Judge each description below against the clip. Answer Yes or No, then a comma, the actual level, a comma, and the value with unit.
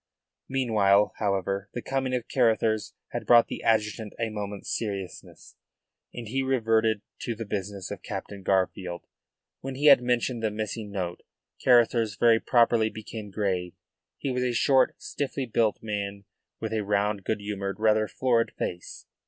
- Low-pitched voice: Yes, low, 110 Hz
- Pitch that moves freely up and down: No, average, 2.8 semitones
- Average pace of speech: Yes, average, 155 wpm